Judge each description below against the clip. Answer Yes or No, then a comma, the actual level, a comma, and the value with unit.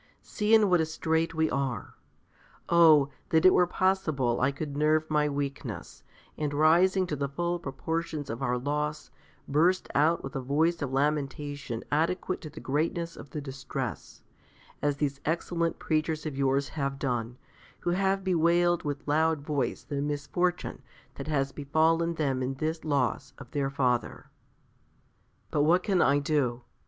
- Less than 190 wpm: Yes, average, 160 wpm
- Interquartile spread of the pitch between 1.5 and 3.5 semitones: Yes, average, 3.1 semitones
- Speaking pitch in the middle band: Yes, medium, 150 Hz